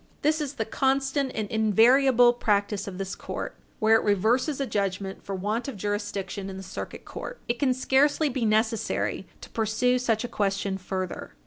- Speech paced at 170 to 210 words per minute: Yes, average, 180 wpm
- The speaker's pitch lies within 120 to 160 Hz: No, high, 220 Hz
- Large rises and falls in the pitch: No, average, 4.4 semitones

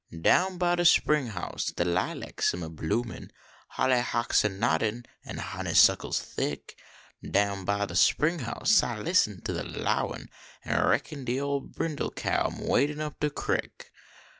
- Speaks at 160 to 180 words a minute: Yes, average, 165 wpm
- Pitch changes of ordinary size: No, wide, 7.0 semitones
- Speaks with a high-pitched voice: No, low, 120 Hz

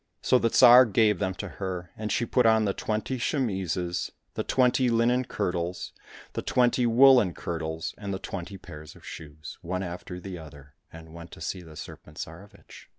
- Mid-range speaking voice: No, very low, 95 Hz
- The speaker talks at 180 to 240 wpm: Yes, average, 185 wpm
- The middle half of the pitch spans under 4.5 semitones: No, wide, 5.5 semitones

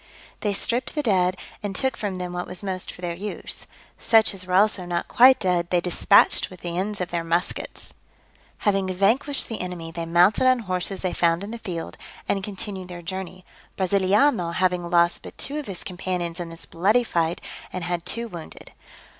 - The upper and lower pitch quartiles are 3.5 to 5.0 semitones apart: No, average, 2.8 semitones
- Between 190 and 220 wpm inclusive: Yes, average, 195 wpm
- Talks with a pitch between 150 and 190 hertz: Yes, medium, 185 Hz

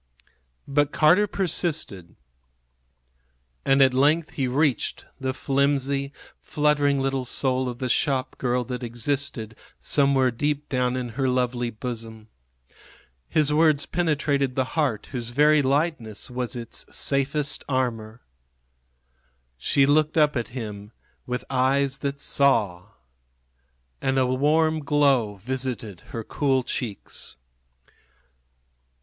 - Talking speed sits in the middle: No, slow, 110 wpm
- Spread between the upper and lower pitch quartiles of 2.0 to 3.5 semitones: Yes, average, 2.8 semitones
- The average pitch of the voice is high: No, low, 135 Hz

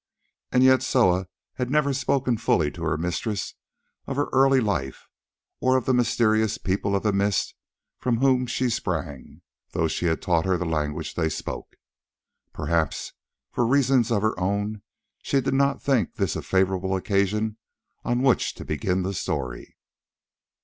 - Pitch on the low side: Yes, low, 105 Hz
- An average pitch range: No, wide, 6.1 semitones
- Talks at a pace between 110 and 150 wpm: No, average, 160 wpm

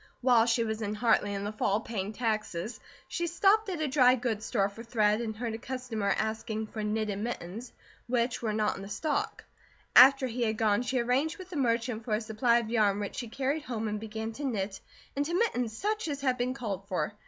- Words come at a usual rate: No, fast, 215 wpm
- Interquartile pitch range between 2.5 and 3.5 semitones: Yes, average, 3.0 semitones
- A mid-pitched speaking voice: No, high, 230 Hz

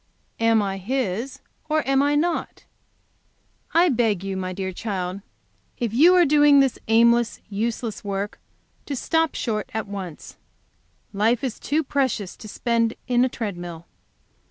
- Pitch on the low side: No, high, 230 Hz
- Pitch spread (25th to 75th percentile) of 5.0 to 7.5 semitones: Yes, wide, 5.4 semitones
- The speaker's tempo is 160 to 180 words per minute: No, average, 150 wpm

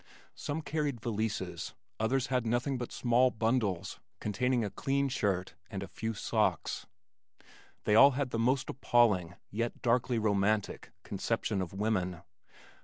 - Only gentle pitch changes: No, average, 3.8 semitones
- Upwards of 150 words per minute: No, slow, 135 wpm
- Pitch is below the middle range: Yes, low, 115 Hz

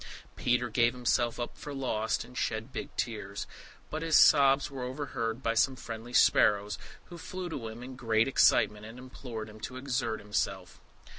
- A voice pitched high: No, low, 120 Hz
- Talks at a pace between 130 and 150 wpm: No, average, 170 wpm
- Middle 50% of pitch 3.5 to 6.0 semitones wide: No, average, 3.0 semitones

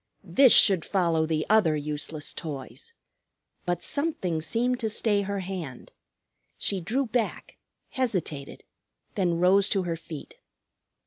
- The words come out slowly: Yes, slow, 125 wpm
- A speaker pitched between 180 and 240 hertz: Yes, medium, 185 Hz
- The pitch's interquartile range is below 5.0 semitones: No, wide, 5.5 semitones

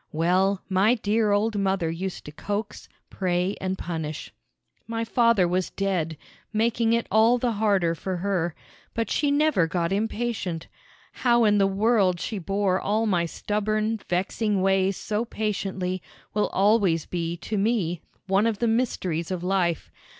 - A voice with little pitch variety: No, average, 3.5 semitones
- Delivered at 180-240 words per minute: No, average, 150 wpm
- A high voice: Yes, high, 195 Hz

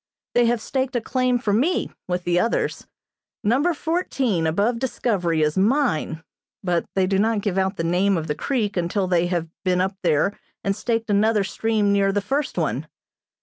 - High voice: Yes, high, 200 Hz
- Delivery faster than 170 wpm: Yes, average, 185 wpm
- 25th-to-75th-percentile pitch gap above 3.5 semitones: Yes, average, 4.9 semitones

